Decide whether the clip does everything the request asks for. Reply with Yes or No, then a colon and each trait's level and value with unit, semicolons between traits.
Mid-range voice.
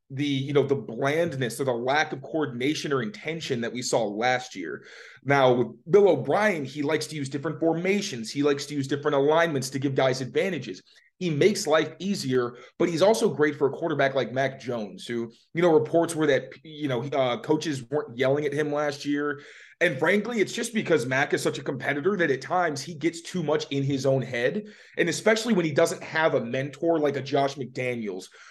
Yes: medium, 145 Hz